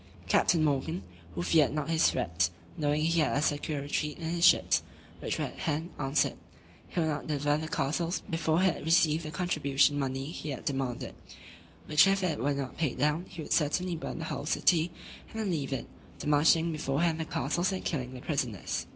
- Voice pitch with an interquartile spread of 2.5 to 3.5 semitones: Yes, average, 2.8 semitones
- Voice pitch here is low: No, medium, 155 Hz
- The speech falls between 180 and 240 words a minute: Yes, average, 200 wpm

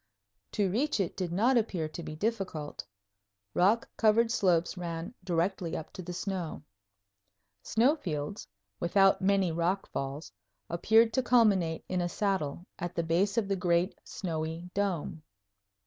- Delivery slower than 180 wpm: Yes, average, 145 wpm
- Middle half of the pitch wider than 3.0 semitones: Yes, average, 3.4 semitones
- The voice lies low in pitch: No, medium, 180 Hz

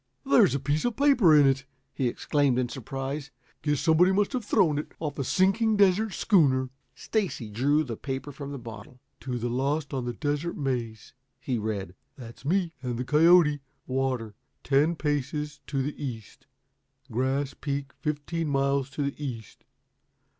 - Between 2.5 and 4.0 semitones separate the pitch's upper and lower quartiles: Yes, average, 3.2 semitones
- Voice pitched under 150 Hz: Yes, medium, 140 Hz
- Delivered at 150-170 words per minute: Yes, average, 165 wpm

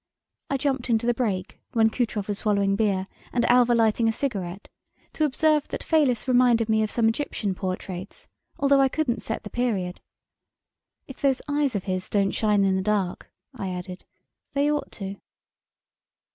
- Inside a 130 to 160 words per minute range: No, average, 170 wpm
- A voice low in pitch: No, high, 225 Hz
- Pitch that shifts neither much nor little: Yes, average, 4.5 semitones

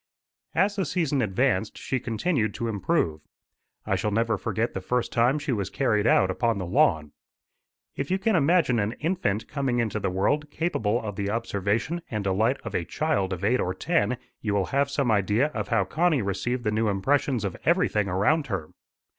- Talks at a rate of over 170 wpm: Yes, average, 190 wpm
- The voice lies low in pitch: Yes, low, 115 Hz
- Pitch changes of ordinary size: No, wide, 5.8 semitones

